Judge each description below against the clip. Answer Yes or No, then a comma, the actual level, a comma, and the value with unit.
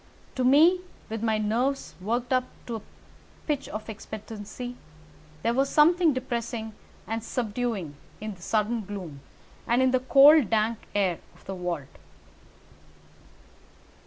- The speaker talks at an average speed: No, slow, 130 wpm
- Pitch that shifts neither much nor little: Yes, average, 3.4 semitones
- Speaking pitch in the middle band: No, high, 230 Hz